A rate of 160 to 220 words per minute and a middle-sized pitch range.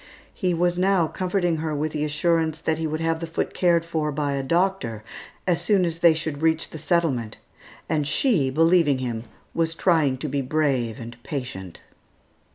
Yes: average, 180 wpm; average, 3.3 semitones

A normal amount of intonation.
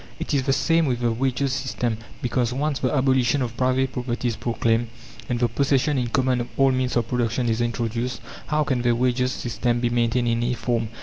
No: narrow, 1.8 semitones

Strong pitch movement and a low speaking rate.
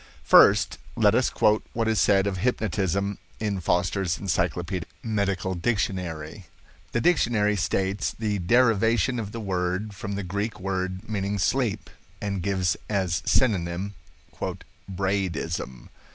No: average, 2.7 semitones; slow, 125 wpm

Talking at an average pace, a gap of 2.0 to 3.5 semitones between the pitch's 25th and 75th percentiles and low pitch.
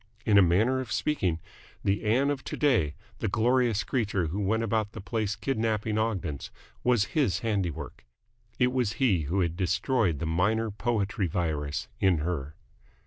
No: average, 160 wpm; average, 4.6 semitones; low, 105 Hz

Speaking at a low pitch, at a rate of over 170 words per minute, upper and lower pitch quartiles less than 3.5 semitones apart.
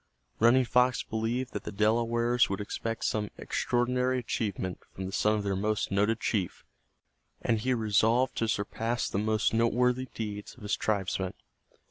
No: low, 110 Hz; average, 155 wpm; average, 2.8 semitones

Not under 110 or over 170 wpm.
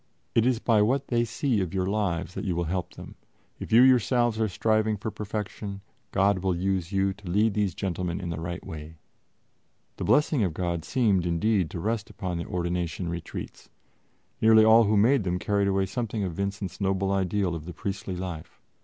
No: average, 195 wpm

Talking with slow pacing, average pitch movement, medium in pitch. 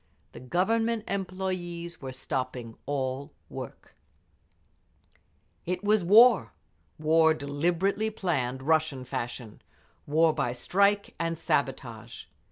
No: slow, 90 wpm; wide, 6.3 semitones; medium, 160 Hz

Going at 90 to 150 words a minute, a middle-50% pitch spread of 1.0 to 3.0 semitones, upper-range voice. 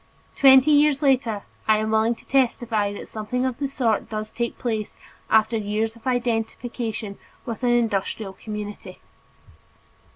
Yes: average, 140 wpm; average, 2.7 semitones; high, 225 Hz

